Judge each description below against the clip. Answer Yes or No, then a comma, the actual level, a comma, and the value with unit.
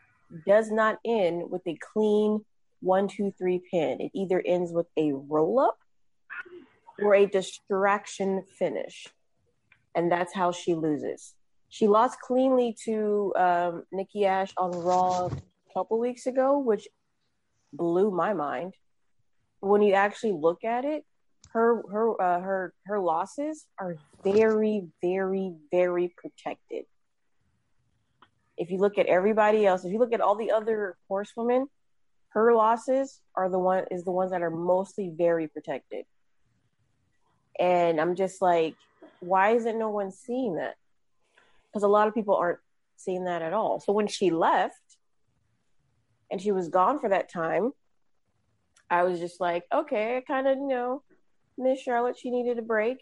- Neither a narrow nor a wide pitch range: Yes, average, 4.1 semitones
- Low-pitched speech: No, high, 195 Hz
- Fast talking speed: No, average, 150 wpm